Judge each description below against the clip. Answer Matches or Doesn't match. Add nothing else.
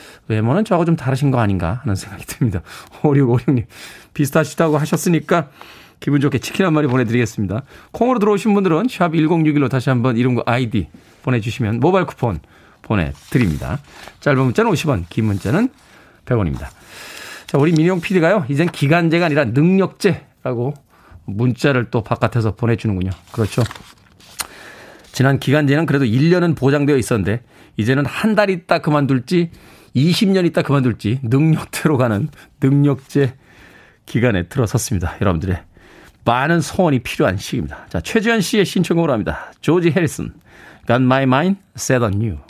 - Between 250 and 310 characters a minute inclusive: Doesn't match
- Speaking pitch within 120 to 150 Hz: Matches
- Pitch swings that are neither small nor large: Doesn't match